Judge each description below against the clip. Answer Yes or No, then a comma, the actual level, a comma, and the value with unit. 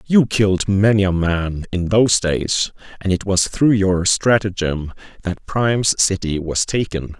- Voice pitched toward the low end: Yes, very low, 95 Hz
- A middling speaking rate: Yes, average, 160 wpm